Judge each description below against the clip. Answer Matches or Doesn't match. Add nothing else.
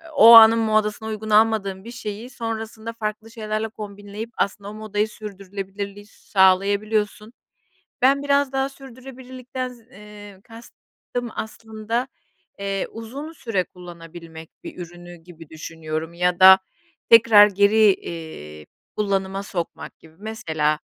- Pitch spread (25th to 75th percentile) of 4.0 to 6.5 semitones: Doesn't match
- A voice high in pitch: Matches